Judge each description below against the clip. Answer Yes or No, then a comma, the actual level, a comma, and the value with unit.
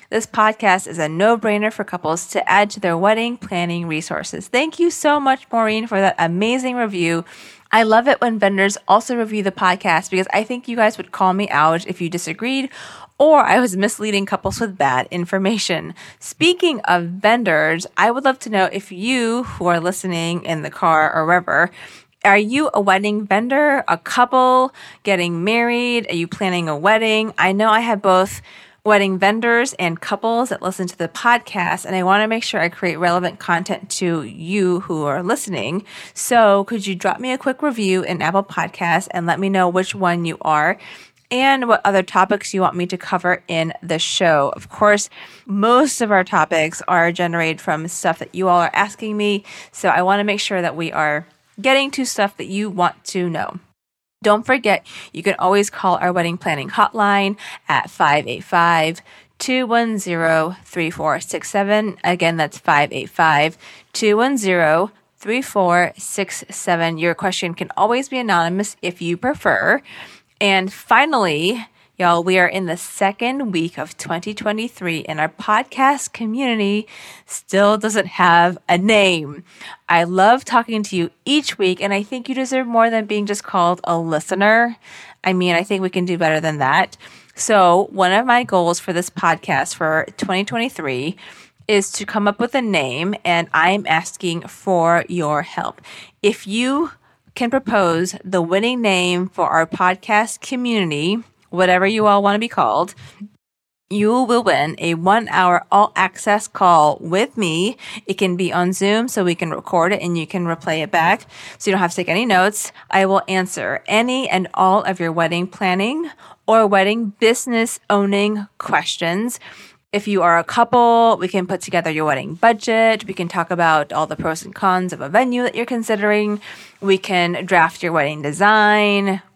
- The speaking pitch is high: Yes, high, 195 Hz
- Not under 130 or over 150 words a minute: No, average, 175 wpm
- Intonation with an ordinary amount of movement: Yes, average, 3.8 semitones